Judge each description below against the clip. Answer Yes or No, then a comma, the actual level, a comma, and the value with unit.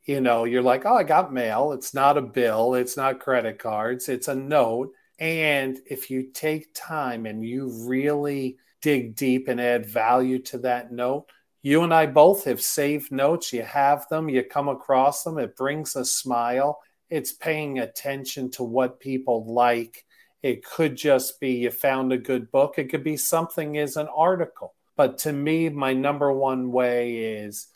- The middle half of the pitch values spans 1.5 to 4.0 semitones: Yes, average, 2.7 semitones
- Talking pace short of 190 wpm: Yes, average, 180 wpm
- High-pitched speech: No, low, 135 Hz